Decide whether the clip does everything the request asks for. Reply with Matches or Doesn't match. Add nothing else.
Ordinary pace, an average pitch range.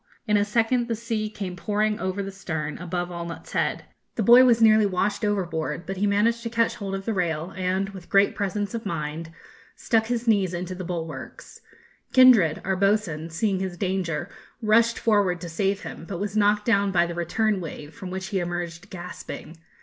Matches